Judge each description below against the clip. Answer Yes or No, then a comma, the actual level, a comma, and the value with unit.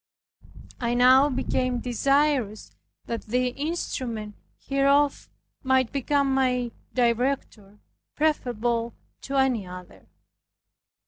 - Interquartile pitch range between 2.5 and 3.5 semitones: Yes, average, 2.8 semitones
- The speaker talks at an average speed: No, slow, 85 wpm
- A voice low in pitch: No, very high, 250 Hz